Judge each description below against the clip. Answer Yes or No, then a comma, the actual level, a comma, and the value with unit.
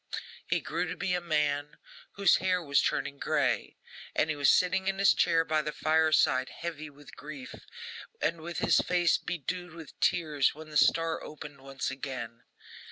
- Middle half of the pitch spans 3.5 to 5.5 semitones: No, average, 3.1 semitones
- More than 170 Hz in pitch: No, medium, 155 Hz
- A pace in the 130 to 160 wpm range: No, average, 170 wpm